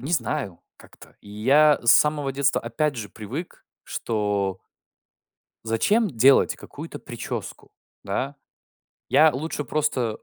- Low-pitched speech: Yes, low, 130 Hz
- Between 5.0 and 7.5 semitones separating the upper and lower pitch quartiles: Yes, wide, 5.5 semitones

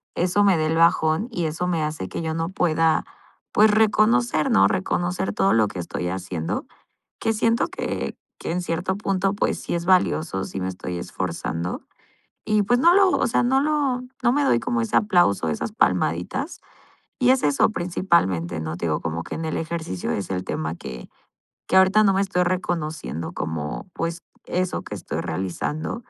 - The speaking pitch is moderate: Yes, medium, 165 Hz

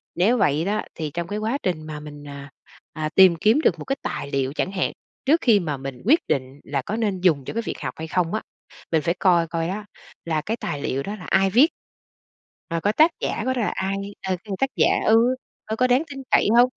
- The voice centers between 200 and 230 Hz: No, medium, 185 Hz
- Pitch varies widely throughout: Yes, wide, 6.1 semitones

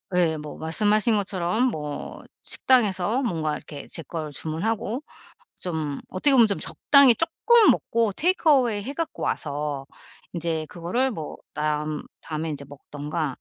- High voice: No, medium, 175 Hz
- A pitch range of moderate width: No, wide, 7.1 semitones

